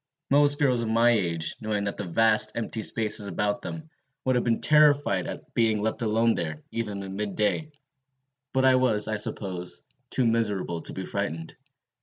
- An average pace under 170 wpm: No, average, 175 wpm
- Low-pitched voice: Yes, low, 110 Hz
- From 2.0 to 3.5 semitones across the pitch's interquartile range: Yes, average, 3.2 semitones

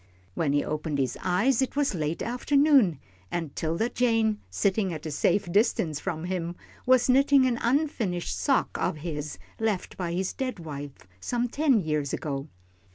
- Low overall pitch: No, medium, 185 Hz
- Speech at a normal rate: Yes, average, 160 wpm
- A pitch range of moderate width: No, wide, 7.9 semitones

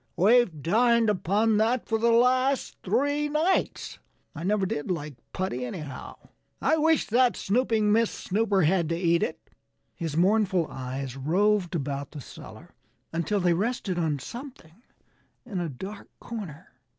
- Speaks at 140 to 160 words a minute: Yes, average, 150 wpm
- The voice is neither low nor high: No, high, 195 Hz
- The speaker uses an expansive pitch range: Yes, wide, 5.9 semitones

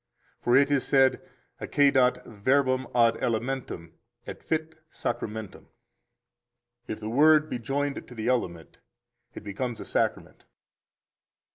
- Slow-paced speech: Yes, slow, 120 wpm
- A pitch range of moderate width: Yes, average, 3.7 semitones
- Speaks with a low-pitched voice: Yes, low, 125 Hz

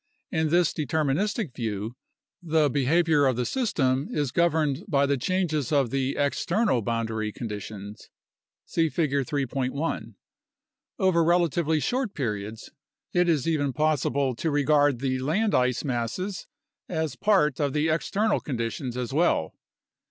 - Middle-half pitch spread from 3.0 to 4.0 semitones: No, average, 4.4 semitones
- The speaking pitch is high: No, medium, 145 Hz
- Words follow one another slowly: Yes, slow, 130 wpm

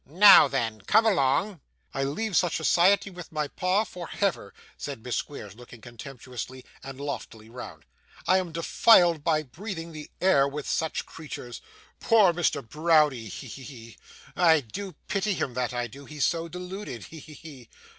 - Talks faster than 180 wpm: No, average, 165 wpm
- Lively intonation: Yes, wide, 5.9 semitones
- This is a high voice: No, medium, 150 Hz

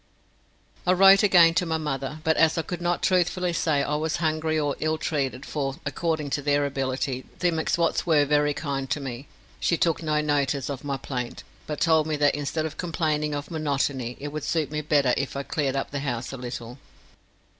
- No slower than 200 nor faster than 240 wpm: Yes, fast, 205 wpm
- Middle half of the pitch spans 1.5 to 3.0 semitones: Yes, narrow, 2.5 semitones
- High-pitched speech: No, medium, 150 Hz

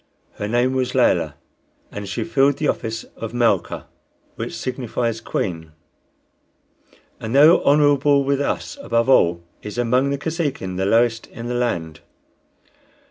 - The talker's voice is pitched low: Yes, low, 120 Hz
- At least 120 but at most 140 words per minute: Yes, slow, 135 wpm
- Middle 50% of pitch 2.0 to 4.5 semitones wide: Yes, average, 4.0 semitones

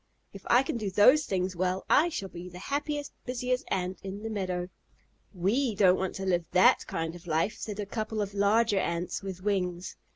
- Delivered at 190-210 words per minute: Yes, average, 200 wpm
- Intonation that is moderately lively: Yes, average, 3.3 semitones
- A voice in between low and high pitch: No, high, 195 Hz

